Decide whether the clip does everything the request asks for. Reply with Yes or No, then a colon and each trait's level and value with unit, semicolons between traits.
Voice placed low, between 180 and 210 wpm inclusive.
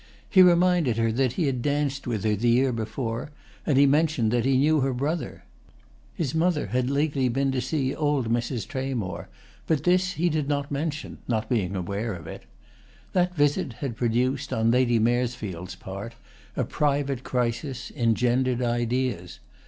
No: low, 130 Hz; average, 165 wpm